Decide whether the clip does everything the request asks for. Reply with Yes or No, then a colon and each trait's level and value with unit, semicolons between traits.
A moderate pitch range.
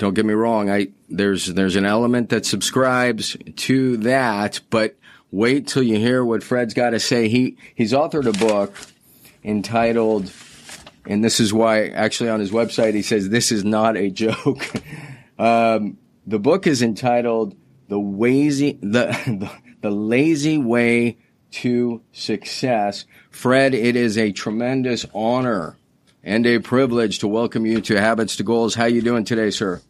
No: narrow, 2.1 semitones